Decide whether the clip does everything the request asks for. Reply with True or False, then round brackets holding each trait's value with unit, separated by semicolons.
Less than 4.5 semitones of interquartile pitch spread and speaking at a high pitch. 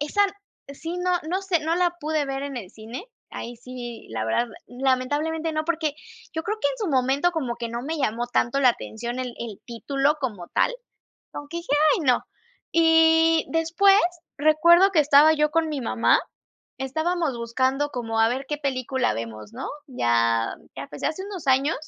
False (5.1 semitones; 280 Hz)